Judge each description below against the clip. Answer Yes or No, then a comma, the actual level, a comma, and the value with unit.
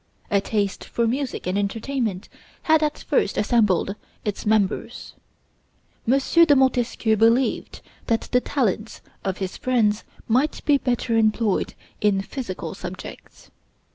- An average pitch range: Yes, average, 4.1 semitones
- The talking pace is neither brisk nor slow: No, slow, 125 wpm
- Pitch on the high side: Yes, high, 225 Hz